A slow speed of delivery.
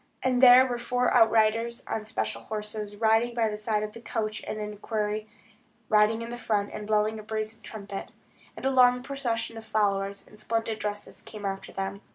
No: average, 190 wpm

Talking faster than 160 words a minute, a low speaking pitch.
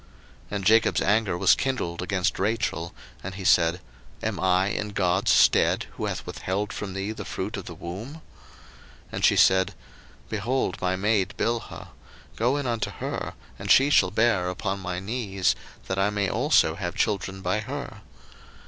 Yes: average, 170 wpm; low, 100 Hz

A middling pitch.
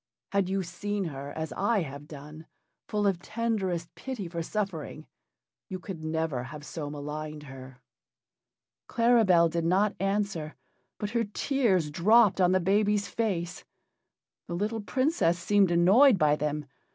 Yes: medium, 180 Hz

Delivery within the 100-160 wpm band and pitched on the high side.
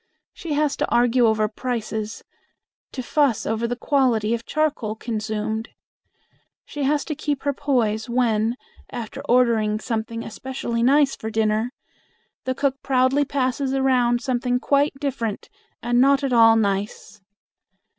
Yes: slow, 135 wpm; high, 245 Hz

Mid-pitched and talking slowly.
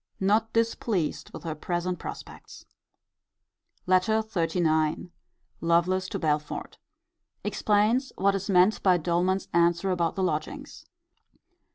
Yes: medium, 180 Hz; slow, 105 wpm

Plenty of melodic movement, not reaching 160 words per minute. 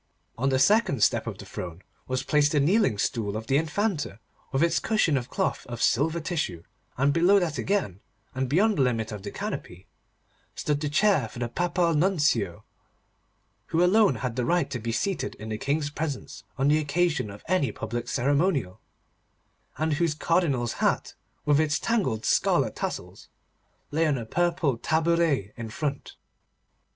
No: wide, 6.0 semitones; average, 170 wpm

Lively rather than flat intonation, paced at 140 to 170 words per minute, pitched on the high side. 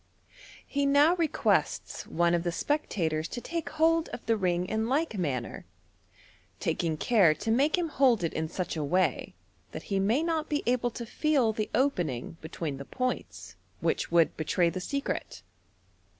Yes: wide, 8.9 semitones; average, 165 wpm; high, 220 Hz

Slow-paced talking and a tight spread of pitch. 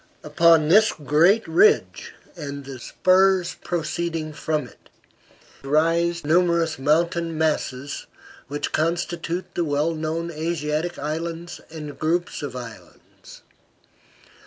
Yes: slow, 105 wpm; narrow, 2.2 semitones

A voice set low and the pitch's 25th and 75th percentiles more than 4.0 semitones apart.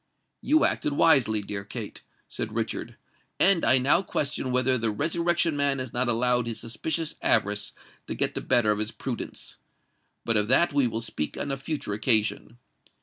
Yes: low, 125 Hz; average, 4.5 semitones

